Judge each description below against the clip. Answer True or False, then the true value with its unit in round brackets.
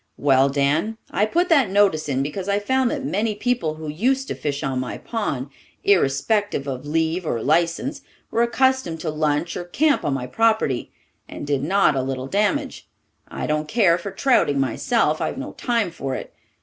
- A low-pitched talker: False (170 Hz)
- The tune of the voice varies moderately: False (7.9 semitones)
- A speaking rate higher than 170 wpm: True (185 wpm)